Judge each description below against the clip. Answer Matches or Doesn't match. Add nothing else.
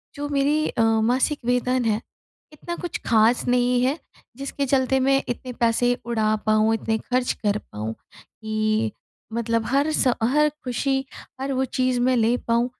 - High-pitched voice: Matches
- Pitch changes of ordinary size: Matches